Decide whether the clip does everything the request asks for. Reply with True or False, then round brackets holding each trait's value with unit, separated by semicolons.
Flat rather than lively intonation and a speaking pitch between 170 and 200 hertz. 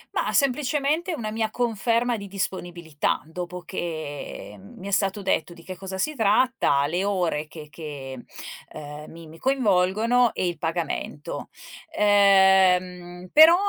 False (5.1 semitones; 185 Hz)